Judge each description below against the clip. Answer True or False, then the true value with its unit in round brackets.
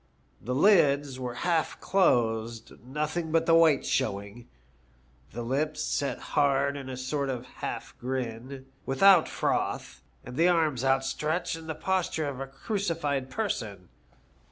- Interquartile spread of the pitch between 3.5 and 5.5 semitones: True (4.1 semitones)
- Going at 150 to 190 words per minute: False (135 wpm)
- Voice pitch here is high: False (140 Hz)